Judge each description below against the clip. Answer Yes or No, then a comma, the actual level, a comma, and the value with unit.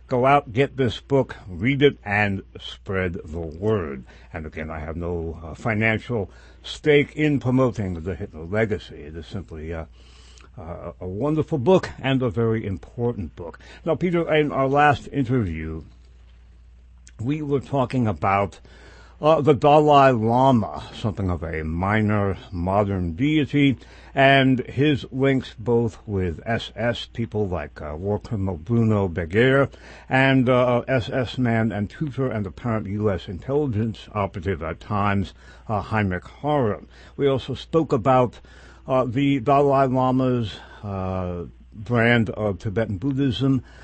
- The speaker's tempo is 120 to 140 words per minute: Yes, slow, 135 wpm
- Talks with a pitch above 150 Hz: No, low, 110 Hz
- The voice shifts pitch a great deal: Yes, wide, 7.3 semitones